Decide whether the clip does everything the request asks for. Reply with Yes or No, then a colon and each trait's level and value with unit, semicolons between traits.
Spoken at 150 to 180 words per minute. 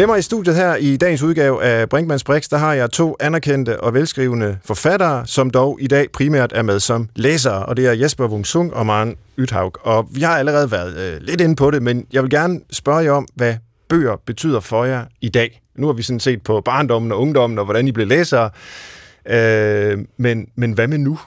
No: fast, 225 wpm